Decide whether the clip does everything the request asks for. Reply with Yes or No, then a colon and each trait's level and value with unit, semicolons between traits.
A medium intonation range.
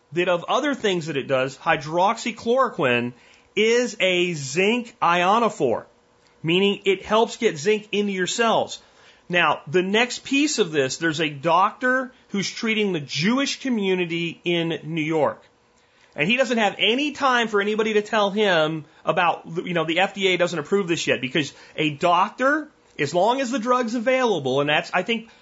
No: wide, 5.8 semitones